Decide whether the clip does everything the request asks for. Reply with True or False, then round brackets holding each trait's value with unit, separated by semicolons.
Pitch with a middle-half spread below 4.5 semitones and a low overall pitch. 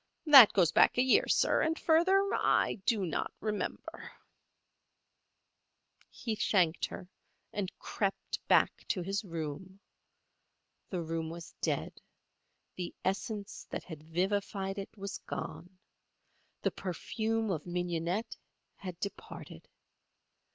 False (3.8 semitones; 195 Hz)